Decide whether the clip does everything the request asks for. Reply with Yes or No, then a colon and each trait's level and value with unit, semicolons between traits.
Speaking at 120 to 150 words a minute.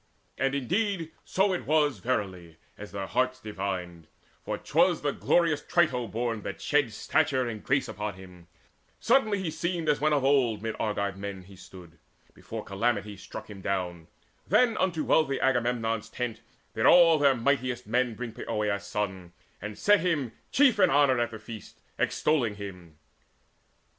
No: average, 160 wpm